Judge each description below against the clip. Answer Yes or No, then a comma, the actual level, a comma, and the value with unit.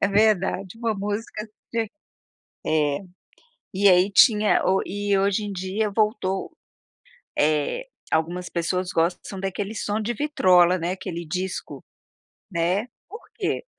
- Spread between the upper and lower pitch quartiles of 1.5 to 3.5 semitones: Yes, average, 2.9 semitones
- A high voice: Yes, high, 195 Hz